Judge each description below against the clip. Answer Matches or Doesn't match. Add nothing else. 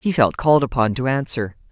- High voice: Doesn't match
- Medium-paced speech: Doesn't match